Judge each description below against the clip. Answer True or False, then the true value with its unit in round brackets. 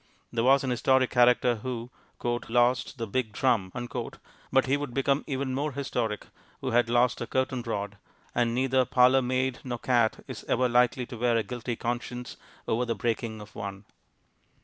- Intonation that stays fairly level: True (1.9 semitones)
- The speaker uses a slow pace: False (170 wpm)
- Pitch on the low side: True (125 Hz)